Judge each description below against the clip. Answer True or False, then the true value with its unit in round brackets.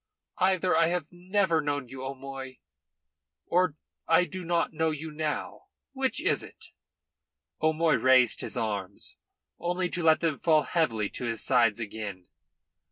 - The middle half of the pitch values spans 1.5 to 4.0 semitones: False (5.0 semitones)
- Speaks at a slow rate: False (145 wpm)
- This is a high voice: False (155 Hz)